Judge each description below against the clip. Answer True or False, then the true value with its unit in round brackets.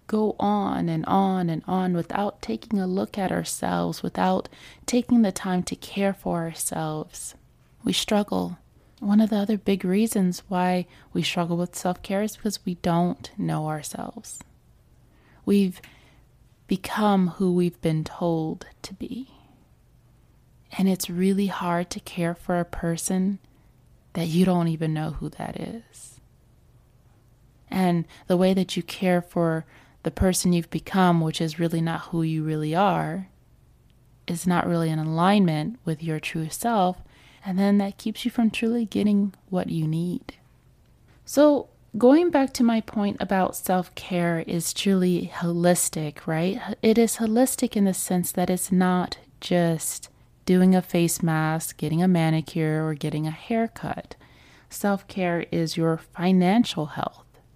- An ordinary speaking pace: True (150 wpm)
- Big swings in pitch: False (3.7 semitones)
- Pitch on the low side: False (180 Hz)